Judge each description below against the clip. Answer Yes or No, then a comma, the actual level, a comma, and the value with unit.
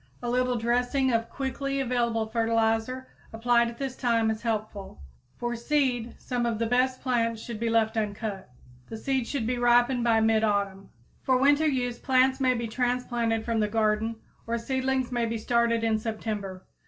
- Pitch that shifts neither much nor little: No, narrow, 2.1 semitones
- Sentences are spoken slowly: No, average, 170 wpm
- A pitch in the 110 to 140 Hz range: No, high, 235 Hz